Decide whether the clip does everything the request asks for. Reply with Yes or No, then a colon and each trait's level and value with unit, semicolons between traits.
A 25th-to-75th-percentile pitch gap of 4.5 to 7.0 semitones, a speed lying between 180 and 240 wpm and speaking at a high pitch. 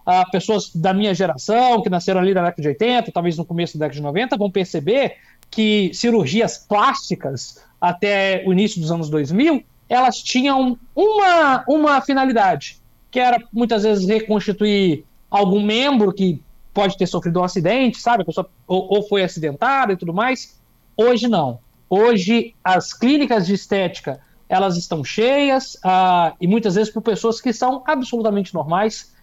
No: average, 4.8 semitones; average, 160 wpm; high, 205 Hz